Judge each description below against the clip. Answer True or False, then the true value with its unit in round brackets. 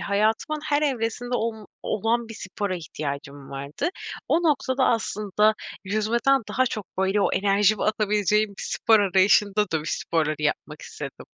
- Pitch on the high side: True (210 Hz)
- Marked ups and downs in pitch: False (3.3 semitones)